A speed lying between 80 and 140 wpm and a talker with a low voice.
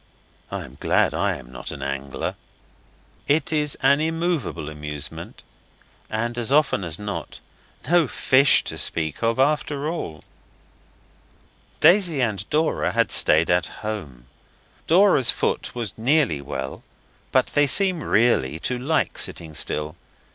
Yes: slow, 135 wpm; low, 115 Hz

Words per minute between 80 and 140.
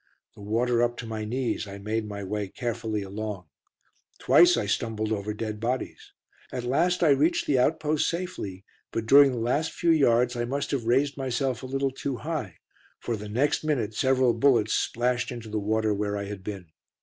No: average, 190 wpm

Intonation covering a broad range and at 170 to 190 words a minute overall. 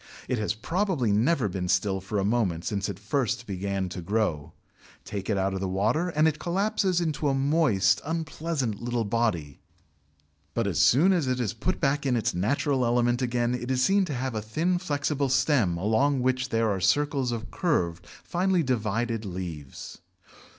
Yes: wide, 6.5 semitones; average, 180 wpm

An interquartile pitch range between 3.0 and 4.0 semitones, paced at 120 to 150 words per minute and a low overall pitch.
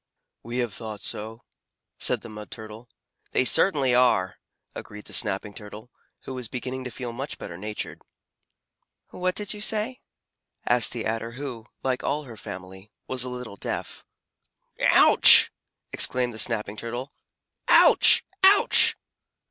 Yes: average, 3.3 semitones; average, 140 wpm; low, 120 Hz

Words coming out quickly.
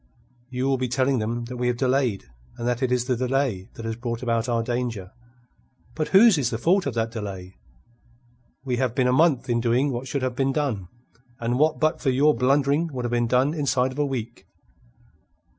Yes: fast, 210 wpm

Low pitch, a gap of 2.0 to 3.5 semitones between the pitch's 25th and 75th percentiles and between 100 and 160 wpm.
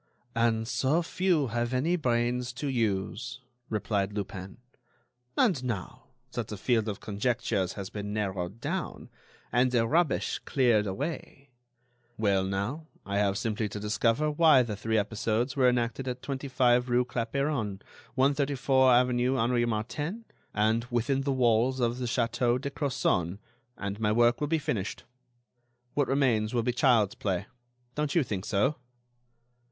No: low, 120 Hz; average, 3.9 semitones; average, 145 wpm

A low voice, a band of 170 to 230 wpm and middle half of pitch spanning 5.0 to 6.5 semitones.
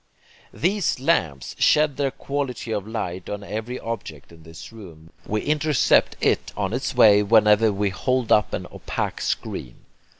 No: low, 110 Hz; average, 155 wpm; wide, 5.4 semitones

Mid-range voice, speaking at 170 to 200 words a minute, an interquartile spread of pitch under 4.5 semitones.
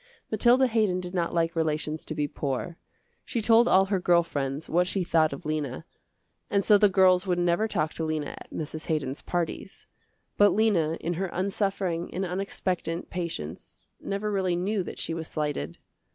Yes: medium, 175 Hz; average, 180 wpm; average, 3.7 semitones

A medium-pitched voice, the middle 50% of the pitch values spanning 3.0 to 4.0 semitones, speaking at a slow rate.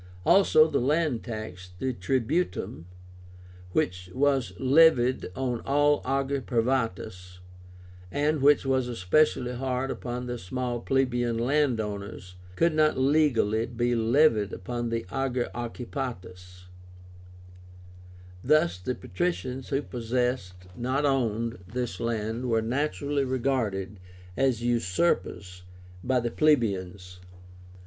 No: low, 125 Hz; average, 3.5 semitones; slow, 105 wpm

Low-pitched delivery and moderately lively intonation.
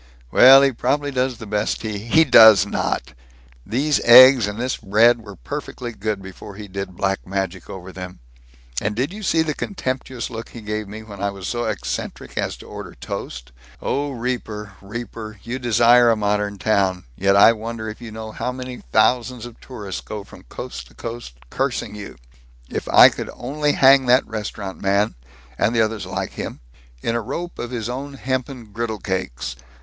Yes: low, 110 Hz; average, 3.8 semitones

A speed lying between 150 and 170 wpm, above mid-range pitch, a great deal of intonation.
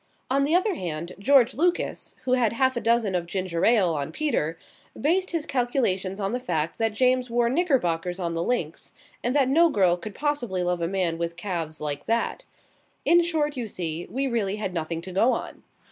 No: average, 200 wpm; high, 215 Hz; wide, 7.2 semitones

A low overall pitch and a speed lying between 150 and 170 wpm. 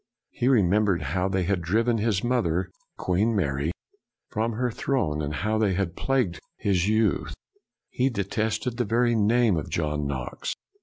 Yes: low, 100 Hz; average, 155 wpm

